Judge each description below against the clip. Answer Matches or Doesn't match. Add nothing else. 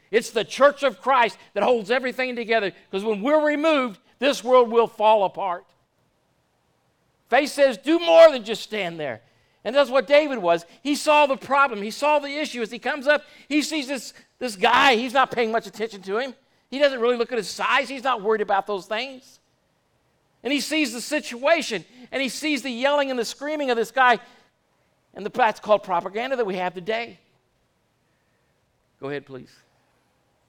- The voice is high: Matches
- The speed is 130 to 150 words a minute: Doesn't match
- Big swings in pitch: Doesn't match